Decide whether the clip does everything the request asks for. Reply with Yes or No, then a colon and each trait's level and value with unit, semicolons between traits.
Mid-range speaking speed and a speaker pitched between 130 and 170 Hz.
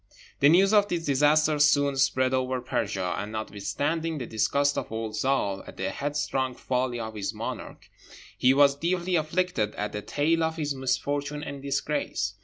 Yes: average, 170 wpm; medium, 140 Hz